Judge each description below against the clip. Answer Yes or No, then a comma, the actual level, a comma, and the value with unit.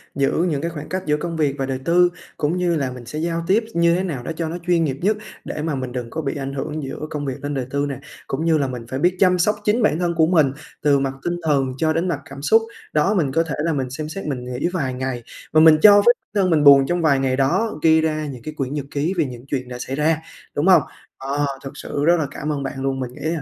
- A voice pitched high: No, medium, 150 Hz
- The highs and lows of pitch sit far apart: No, average, 3.7 semitones